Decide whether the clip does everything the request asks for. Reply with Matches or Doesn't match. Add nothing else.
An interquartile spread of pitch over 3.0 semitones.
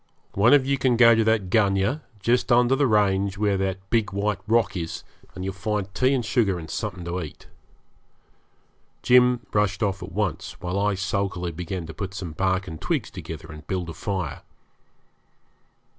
Matches